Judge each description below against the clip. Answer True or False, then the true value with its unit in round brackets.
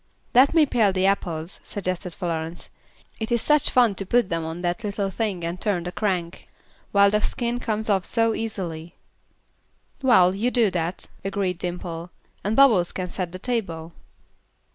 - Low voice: False (195 Hz)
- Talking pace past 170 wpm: False (165 wpm)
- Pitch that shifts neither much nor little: True (4.2 semitones)